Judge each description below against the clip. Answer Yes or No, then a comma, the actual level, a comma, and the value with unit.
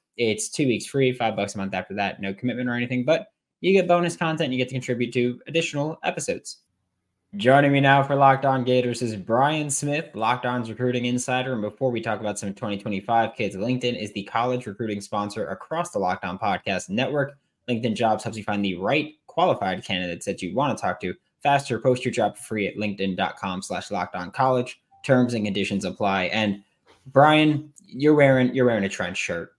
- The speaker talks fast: No, average, 195 wpm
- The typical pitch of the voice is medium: No, low, 125 Hz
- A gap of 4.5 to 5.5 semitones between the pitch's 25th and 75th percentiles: Yes, average, 5.0 semitones